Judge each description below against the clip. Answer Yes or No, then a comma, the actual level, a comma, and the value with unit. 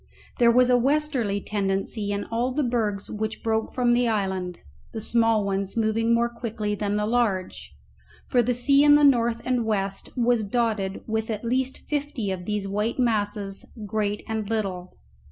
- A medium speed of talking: Yes, average, 170 wpm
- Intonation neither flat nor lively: Yes, average, 3.0 semitones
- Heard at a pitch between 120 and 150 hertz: No, high, 220 Hz